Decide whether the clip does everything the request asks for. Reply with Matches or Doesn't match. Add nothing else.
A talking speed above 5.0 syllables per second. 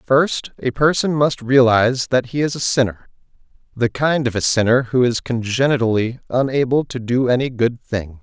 Doesn't match